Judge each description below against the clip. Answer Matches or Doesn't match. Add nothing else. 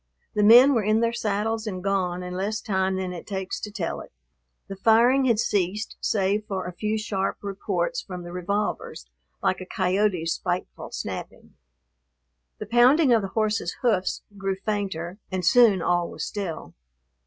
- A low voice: Doesn't match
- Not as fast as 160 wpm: Doesn't match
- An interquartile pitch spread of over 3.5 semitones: Doesn't match